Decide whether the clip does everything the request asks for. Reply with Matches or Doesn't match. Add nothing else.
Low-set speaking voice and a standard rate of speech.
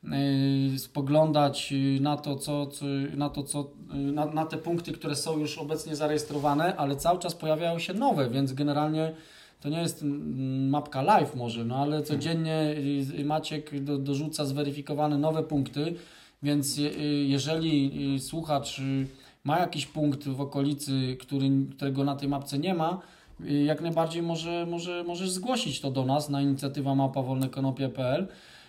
Doesn't match